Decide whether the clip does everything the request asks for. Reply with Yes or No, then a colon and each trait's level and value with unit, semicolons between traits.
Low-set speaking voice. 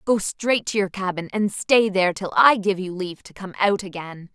No: high, 195 Hz